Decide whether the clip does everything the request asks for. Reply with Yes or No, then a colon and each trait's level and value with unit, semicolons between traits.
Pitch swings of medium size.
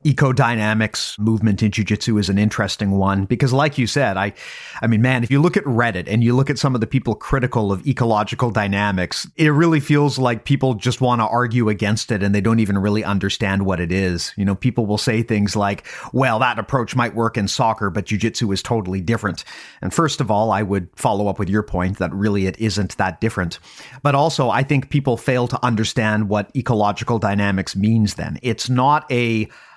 Yes: average, 3.6 semitones